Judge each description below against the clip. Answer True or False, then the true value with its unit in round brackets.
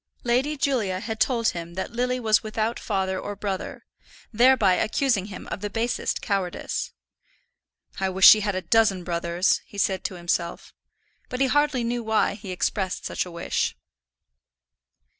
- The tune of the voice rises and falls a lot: False (4.0 semitones)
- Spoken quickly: False (160 wpm)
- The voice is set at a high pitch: True (205 Hz)